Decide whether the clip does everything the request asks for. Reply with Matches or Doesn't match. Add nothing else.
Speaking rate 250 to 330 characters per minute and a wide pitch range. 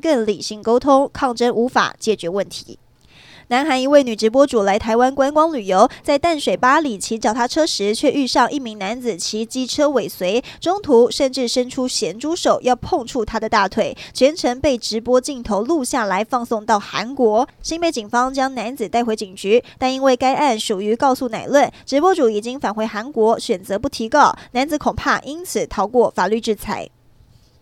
Doesn't match